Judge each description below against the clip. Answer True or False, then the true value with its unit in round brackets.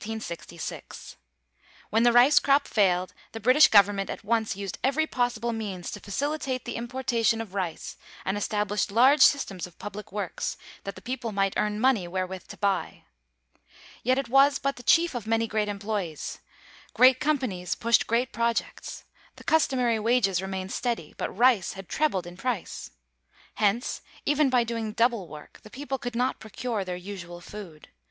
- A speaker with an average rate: True (160 wpm)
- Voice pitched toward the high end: True (225 Hz)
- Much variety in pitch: False (4.3 semitones)